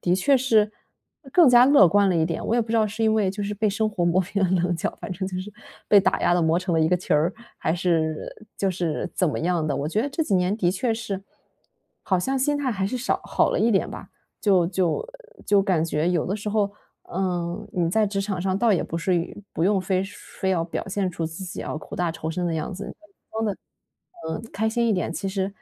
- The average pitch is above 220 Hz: No, high, 190 Hz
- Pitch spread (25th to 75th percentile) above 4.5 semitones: No, average, 3.4 semitones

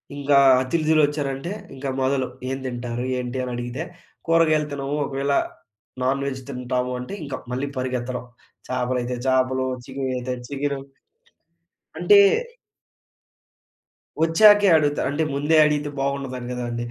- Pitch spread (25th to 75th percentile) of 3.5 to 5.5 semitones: No, narrow, 2.5 semitones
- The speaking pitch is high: No, low, 135 Hz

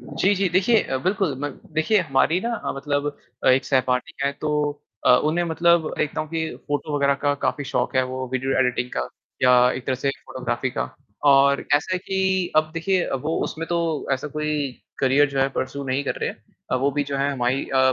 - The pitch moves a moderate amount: Yes, average, 3.7 semitones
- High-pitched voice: No, medium, 145 Hz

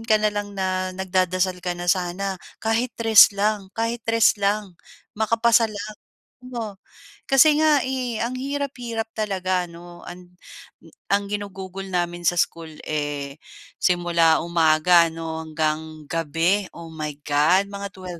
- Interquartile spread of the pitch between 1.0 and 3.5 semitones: No, average, 4.0 semitones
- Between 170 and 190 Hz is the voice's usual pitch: Yes, medium, 185 Hz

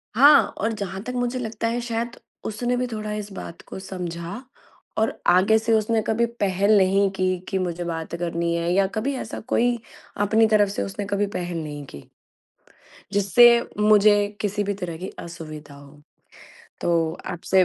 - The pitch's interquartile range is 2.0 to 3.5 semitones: No, average, 4.2 semitones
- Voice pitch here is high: Yes, high, 200 Hz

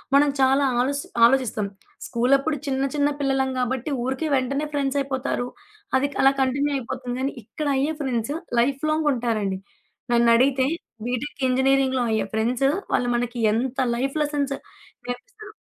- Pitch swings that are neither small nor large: No, narrow, 2.3 semitones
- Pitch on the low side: No, very high, 265 Hz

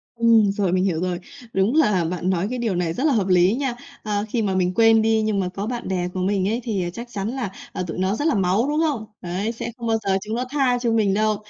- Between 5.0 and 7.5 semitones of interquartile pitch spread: No, average, 3.8 semitones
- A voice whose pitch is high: Yes, high, 210 Hz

